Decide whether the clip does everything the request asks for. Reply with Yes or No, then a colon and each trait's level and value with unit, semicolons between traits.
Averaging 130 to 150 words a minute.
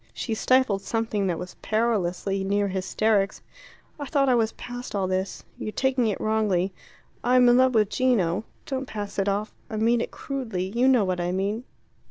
No: average, 185 wpm